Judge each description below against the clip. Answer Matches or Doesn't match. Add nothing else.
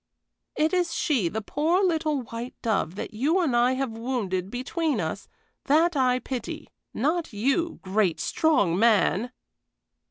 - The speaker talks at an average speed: Matches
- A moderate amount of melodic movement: Doesn't match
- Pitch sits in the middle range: Doesn't match